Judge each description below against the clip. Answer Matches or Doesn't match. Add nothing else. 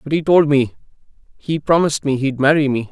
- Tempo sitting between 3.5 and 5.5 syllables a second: Doesn't match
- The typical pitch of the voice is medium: Matches